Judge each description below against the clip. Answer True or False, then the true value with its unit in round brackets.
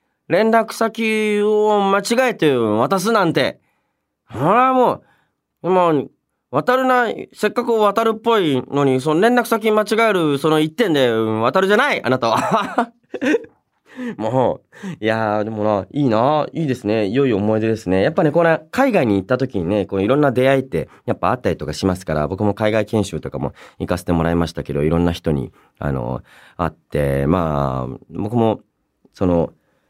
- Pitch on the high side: False (135 Hz)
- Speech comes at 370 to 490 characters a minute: False (320 characters per minute)